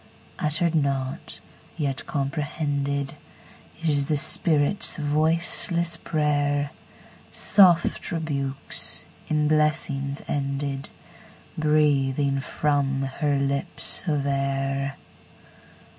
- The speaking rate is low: Yes, slow, 65 wpm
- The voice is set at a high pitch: No, medium, 145 Hz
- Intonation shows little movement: Yes, narrow, 1.9 semitones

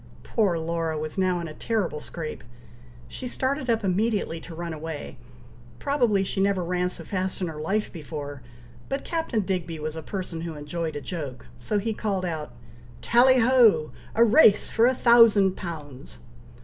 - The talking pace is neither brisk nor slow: Yes, average, 170 wpm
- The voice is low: No, medium, 180 Hz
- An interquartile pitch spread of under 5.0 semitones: No, wide, 5.5 semitones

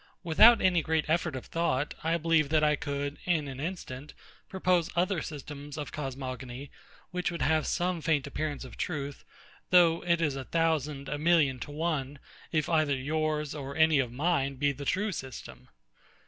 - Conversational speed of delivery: Yes, average, 175 wpm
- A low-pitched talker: No, medium, 150 Hz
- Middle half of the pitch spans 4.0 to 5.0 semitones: No, average, 3.1 semitones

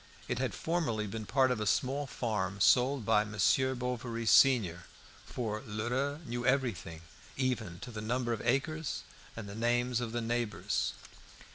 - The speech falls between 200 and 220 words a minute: No, average, 155 wpm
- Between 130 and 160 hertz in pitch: No, low, 120 Hz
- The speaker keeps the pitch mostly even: No, average, 3.2 semitones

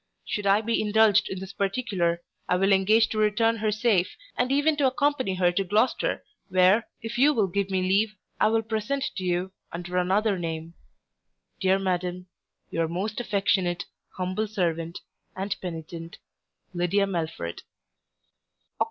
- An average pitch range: Yes, average, 3.4 semitones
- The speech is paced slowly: No, average, 150 wpm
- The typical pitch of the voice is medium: No, high, 195 Hz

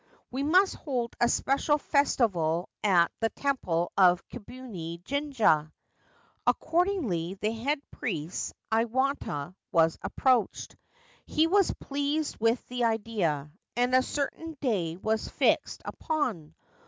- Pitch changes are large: Yes, wide, 8.1 semitones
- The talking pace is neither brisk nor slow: No, slow, 115 wpm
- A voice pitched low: No, high, 235 Hz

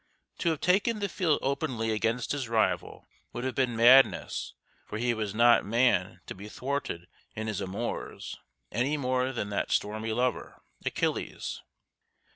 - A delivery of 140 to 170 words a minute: Yes, average, 150 wpm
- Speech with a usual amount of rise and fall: Yes, average, 3.5 semitones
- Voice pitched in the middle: No, low, 120 Hz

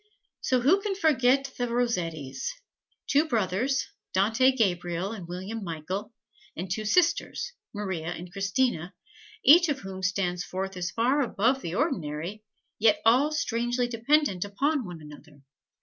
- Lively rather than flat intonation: Yes, wide, 6.6 semitones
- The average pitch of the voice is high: Yes, high, 215 Hz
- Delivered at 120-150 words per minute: Yes, slow, 135 wpm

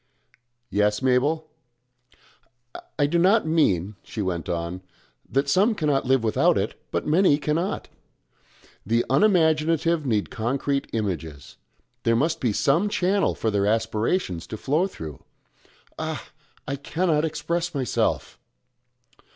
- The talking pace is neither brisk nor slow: No, slow, 120 wpm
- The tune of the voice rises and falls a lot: Yes, wide, 7.2 semitones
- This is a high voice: No, medium, 140 Hz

